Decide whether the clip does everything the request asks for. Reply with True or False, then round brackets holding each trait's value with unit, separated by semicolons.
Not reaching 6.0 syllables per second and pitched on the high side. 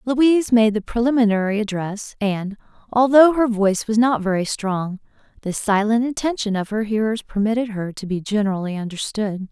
True (5.3 syllables/s; 215 Hz)